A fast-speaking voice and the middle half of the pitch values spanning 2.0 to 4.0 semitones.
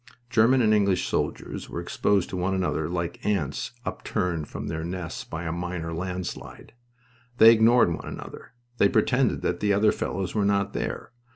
No: average, 170 wpm; average, 3.6 semitones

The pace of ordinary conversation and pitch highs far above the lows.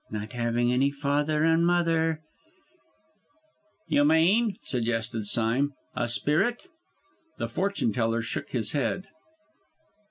No: slow, 115 wpm; wide, 6.1 semitones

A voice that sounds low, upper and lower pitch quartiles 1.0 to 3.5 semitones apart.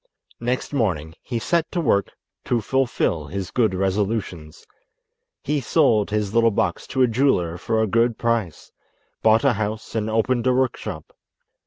No: low, 110 Hz; average, 4.1 semitones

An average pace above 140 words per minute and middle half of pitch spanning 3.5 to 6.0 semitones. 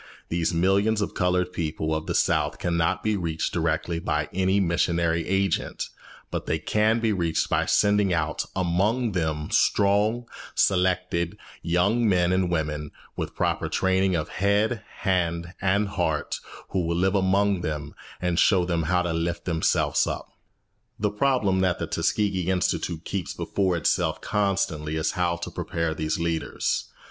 No: average, 155 wpm; average, 3.0 semitones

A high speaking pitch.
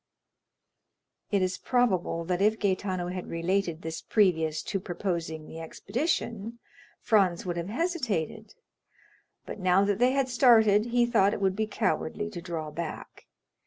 Yes: high, 195 Hz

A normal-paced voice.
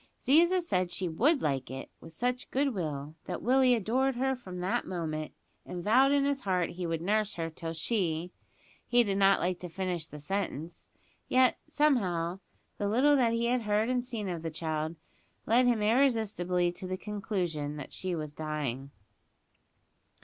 Yes: average, 170 wpm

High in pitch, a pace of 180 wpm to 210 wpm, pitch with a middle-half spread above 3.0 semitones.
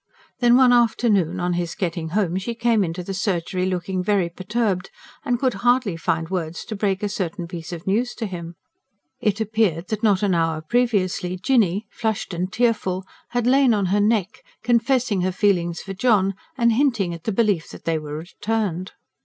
Yes: high, 195 Hz; average, 185 wpm; average, 4.3 semitones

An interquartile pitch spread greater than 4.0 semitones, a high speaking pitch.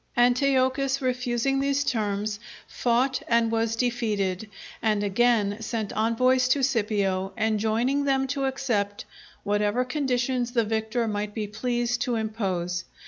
No: average, 3.3 semitones; high, 235 Hz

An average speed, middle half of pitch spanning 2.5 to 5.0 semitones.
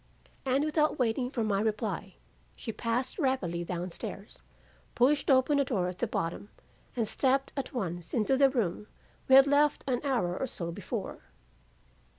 No: average, 165 wpm; wide, 5.4 semitones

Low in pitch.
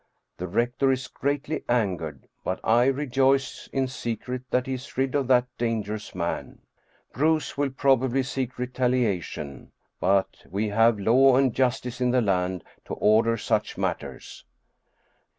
Yes: low, 125 Hz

